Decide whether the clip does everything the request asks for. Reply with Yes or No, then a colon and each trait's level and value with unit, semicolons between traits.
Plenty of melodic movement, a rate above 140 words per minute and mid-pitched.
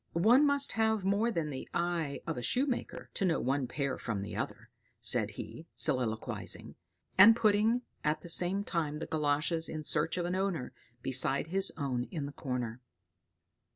Yes: wide, 6.1 semitones; average, 170 wpm; medium, 165 Hz